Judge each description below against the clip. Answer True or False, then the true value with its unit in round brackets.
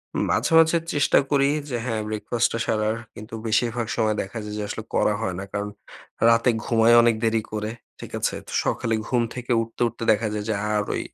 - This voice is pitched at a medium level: False (115 Hz)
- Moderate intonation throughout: False (1.7 semitones)